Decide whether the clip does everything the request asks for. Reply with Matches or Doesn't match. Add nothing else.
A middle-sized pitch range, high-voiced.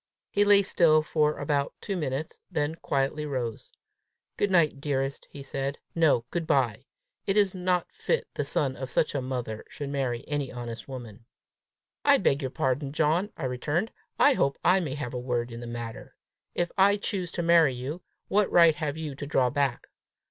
Doesn't match